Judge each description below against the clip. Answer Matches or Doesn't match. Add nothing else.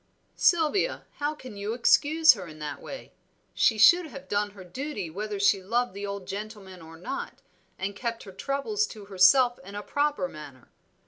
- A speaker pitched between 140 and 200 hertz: Doesn't match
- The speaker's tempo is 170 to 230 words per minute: Matches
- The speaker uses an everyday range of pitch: Doesn't match